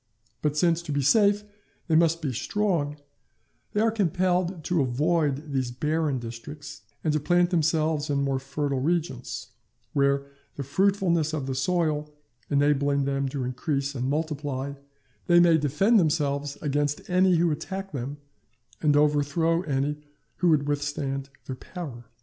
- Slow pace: No, average, 145 wpm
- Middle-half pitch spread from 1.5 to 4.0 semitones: Yes, average, 3.3 semitones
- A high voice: No, medium, 150 Hz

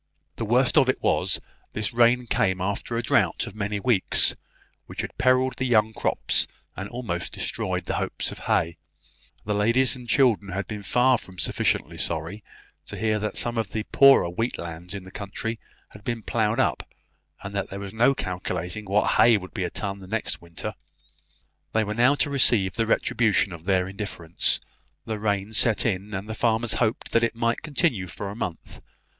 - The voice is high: No, low, 105 Hz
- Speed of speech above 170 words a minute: Yes, average, 190 wpm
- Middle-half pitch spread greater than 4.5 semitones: No, average, 3.5 semitones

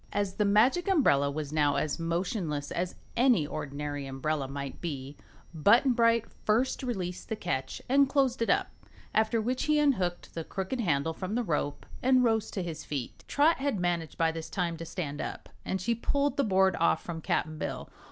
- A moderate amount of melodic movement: No, wide, 7.3 semitones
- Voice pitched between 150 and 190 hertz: Yes, medium, 185 Hz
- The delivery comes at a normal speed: Yes, average, 190 wpm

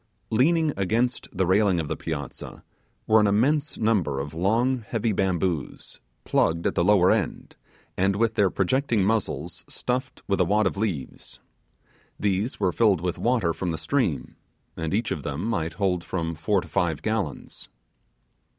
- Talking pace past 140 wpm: Yes, average, 160 wpm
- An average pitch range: Yes, average, 4.8 semitones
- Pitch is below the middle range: Yes, very low, 95 Hz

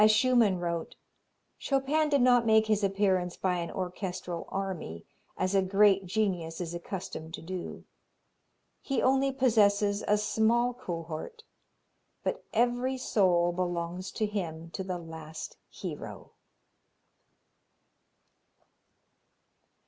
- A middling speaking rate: No, slow, 110 wpm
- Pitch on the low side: No, high, 195 Hz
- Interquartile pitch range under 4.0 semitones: No, average, 4.3 semitones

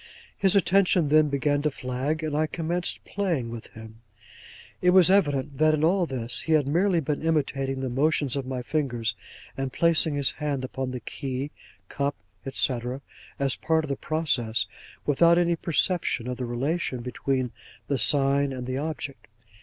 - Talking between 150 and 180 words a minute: Yes, average, 170 wpm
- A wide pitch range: No, average, 3.6 semitones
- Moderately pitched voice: Yes, medium, 145 Hz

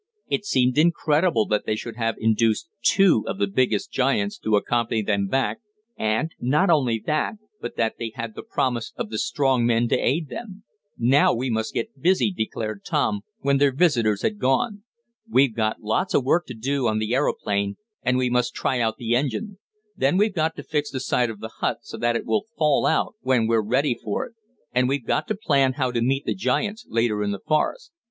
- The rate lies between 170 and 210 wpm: Yes, fast, 205 wpm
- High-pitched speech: No, low, 125 Hz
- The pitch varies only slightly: No, average, 5.1 semitones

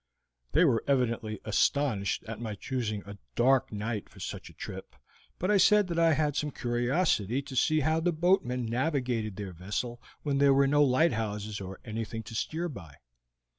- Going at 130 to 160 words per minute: No, average, 175 wpm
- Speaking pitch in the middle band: No, low, 125 Hz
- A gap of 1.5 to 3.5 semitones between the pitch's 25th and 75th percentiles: No, average, 5.3 semitones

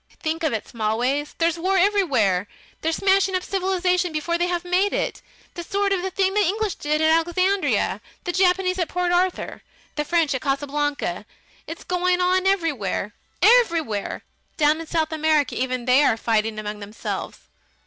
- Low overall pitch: No, very high, 335 Hz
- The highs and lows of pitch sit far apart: No, average, 4.4 semitones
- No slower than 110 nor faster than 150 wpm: No, average, 170 wpm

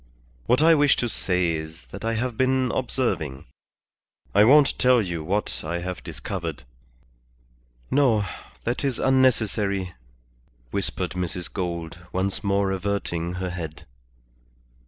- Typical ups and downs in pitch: No, wide, 5.9 semitones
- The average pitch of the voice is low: Yes, very low, 95 Hz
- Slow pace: Yes, slow, 130 wpm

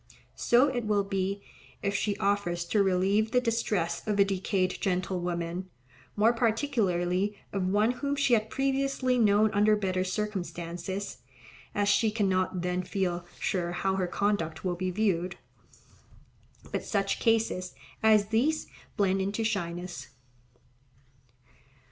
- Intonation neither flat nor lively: Yes, average, 3.1 semitones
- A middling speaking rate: No, slow, 130 wpm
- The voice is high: Yes, high, 200 Hz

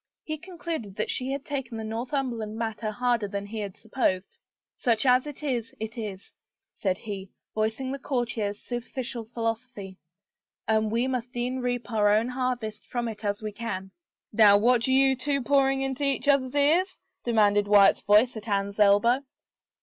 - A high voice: Yes, high, 230 Hz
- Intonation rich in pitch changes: No, average, 3.5 semitones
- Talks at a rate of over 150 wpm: Yes, average, 180 wpm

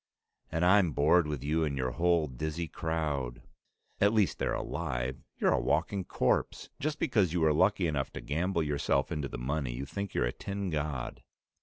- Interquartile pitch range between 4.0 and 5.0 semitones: Yes, average, 4.3 semitones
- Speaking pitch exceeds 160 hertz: No, very low, 80 Hz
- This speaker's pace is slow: No, average, 185 wpm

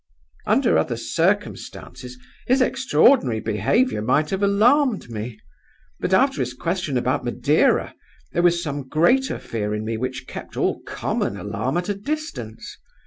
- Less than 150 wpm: Yes, average, 140 wpm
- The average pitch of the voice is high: No, medium, 145 Hz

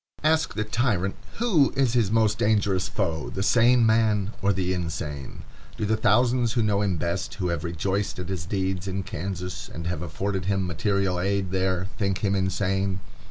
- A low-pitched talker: Yes, very low, 95 Hz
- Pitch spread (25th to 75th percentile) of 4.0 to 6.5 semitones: No, average, 3.0 semitones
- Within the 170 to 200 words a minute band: Yes, average, 180 wpm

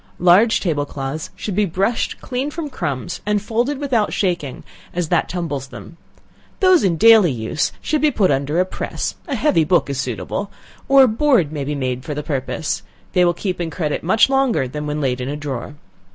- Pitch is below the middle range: No, medium, 175 Hz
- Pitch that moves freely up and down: Yes, wide, 7.7 semitones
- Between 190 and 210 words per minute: Yes, average, 200 wpm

